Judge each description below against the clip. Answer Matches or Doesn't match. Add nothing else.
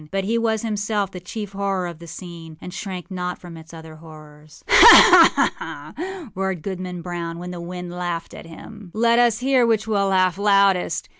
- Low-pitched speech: Doesn't match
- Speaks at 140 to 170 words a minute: Doesn't match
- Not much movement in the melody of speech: Doesn't match